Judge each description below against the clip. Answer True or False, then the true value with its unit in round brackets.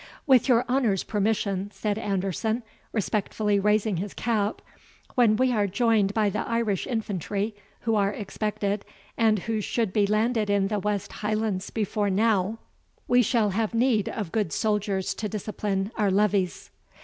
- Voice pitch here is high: True (210 Hz)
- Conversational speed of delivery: True (150 wpm)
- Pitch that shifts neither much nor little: False (1.9 semitones)